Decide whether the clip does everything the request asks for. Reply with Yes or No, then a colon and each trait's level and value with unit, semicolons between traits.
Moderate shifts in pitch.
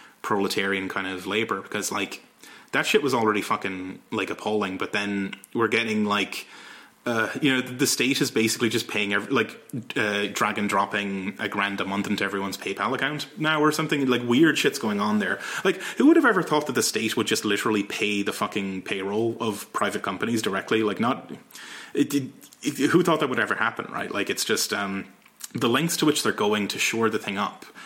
Yes: average, 3.8 semitones